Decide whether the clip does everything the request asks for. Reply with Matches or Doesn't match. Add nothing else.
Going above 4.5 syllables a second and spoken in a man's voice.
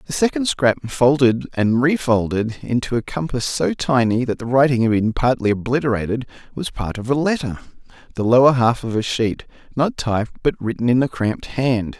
Matches